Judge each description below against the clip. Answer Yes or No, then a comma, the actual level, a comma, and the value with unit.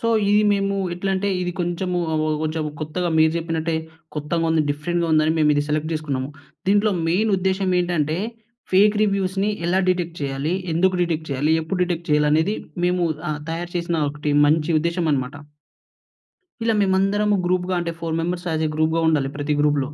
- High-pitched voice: No, medium, 170 Hz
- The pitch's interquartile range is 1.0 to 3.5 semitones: Yes, average, 3.1 semitones